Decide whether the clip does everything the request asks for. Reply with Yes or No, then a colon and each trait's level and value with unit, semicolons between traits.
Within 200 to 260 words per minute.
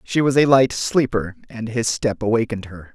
Yes: fast, 205 wpm